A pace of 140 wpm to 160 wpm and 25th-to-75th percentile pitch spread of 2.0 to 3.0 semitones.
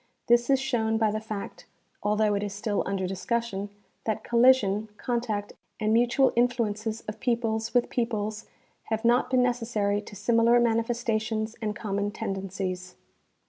Yes: average, 145 wpm; narrow, 2.4 semitones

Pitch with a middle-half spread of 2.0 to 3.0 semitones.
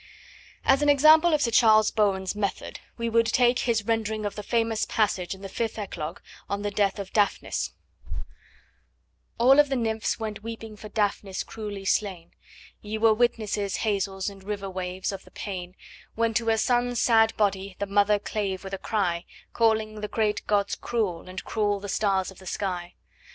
Yes: narrow, 2.5 semitones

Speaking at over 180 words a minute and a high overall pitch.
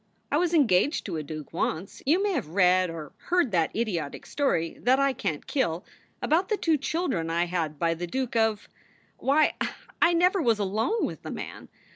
Yes: average, 195 wpm; high, 220 Hz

